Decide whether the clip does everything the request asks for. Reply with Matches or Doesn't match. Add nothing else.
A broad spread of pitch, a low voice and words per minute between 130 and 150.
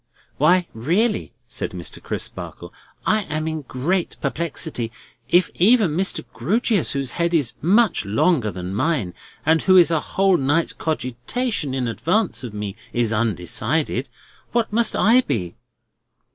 Doesn't match